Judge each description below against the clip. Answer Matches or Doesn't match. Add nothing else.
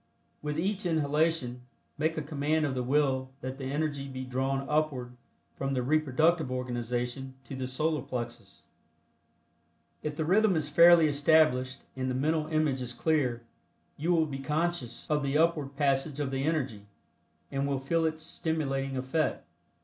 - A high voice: Doesn't match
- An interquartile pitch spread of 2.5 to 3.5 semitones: Matches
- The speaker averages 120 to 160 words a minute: Matches